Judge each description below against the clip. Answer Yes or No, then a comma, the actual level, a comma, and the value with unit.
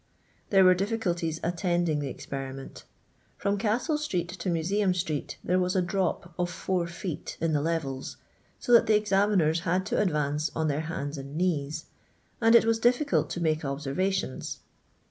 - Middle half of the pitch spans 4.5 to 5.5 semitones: No, average, 4.0 semitones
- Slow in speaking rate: No, average, 165 wpm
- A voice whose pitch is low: No, medium, 175 Hz